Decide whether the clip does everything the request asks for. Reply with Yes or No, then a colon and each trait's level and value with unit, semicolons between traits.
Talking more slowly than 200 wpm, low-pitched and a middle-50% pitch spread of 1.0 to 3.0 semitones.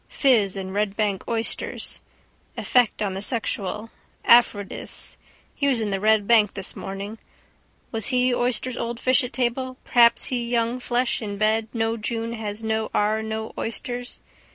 No: average, 155 wpm; high, 225 Hz; narrow, 2.6 semitones